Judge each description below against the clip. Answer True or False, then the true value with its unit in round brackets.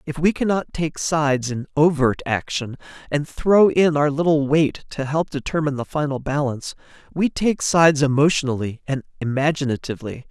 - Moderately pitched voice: True (145 Hz)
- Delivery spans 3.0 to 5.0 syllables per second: False (5.4 syllables/s)